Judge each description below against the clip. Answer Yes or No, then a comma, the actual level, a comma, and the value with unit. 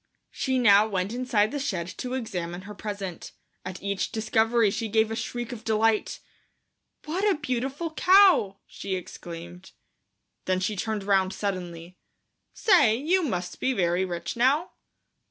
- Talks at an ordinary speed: Yes, average, 145 wpm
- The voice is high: Yes, high, 215 Hz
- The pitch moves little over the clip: No, average, 5.1 semitones